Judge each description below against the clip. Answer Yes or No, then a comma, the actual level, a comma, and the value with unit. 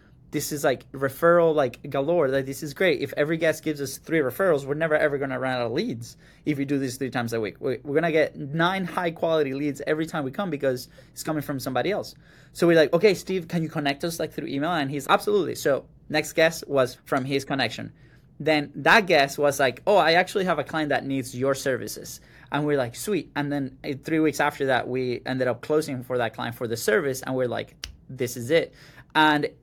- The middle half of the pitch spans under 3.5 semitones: Yes, average, 3.0 semitones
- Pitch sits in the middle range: Yes, medium, 145 Hz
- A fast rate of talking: Yes, fast, 230 wpm